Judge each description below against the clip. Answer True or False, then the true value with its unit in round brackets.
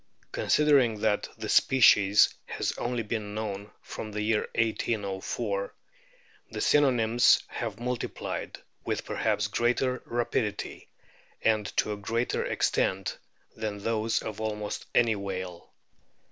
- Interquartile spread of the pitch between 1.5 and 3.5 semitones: True (2.5 semitones)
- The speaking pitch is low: True (110 Hz)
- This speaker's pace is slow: True (115 wpm)